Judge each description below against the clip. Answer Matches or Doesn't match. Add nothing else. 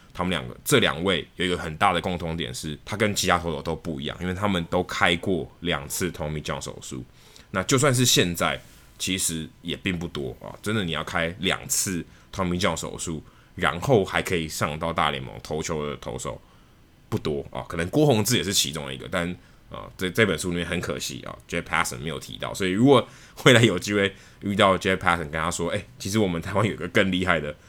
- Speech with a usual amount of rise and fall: Matches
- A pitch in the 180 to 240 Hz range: Doesn't match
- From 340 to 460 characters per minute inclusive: Matches